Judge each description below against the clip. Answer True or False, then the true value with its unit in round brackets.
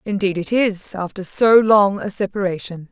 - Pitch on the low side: False (200 Hz)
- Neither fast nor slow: True (165 wpm)